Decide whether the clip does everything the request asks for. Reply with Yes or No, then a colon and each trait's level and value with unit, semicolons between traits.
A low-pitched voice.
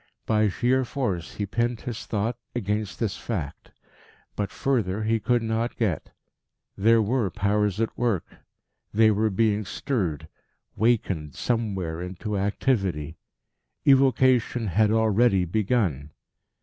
Yes: low, 110 Hz